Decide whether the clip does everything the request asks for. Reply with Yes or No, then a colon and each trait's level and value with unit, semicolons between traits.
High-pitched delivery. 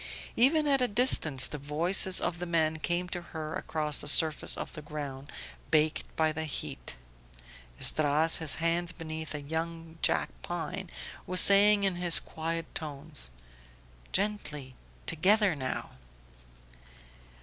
No: medium, 160 Hz